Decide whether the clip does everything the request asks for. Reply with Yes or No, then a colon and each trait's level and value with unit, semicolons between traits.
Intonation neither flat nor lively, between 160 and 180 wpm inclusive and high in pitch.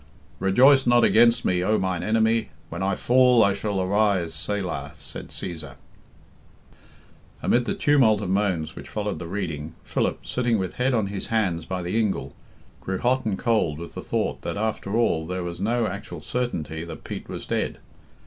No: average, 4.5 semitones; average, 175 wpm; low, 100 Hz